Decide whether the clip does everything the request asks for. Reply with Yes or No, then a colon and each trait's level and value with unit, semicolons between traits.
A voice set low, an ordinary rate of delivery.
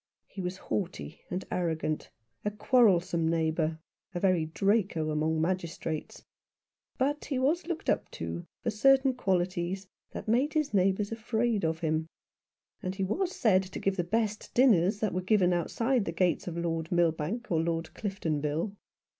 No: medium, 185 Hz; average, 155 wpm